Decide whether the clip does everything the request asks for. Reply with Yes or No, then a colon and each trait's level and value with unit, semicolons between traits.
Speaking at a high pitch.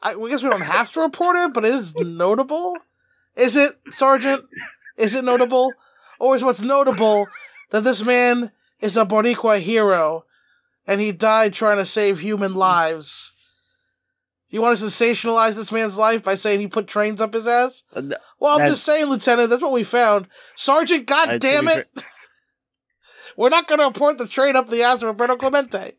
Yes: high, 240 Hz